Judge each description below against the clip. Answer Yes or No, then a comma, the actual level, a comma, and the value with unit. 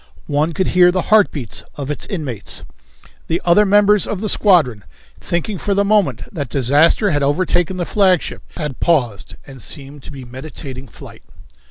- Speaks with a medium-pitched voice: Yes, medium, 165 Hz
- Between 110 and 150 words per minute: No, average, 165 wpm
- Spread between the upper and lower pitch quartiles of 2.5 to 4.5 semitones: No, wide, 5.5 semitones